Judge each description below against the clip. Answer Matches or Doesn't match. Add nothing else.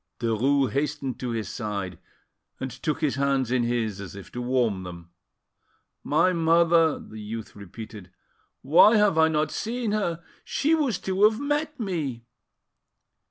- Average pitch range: Doesn't match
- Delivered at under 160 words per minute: Matches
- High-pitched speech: Doesn't match